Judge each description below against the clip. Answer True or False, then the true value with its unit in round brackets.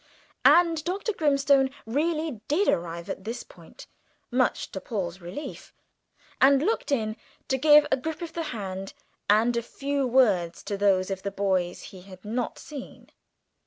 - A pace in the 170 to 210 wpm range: False (160 wpm)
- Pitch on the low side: False (240 Hz)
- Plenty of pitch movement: True (7.3 semitones)